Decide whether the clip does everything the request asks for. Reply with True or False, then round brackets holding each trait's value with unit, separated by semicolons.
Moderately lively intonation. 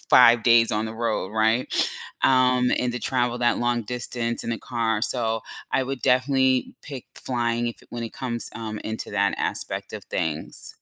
False (1.9 semitones)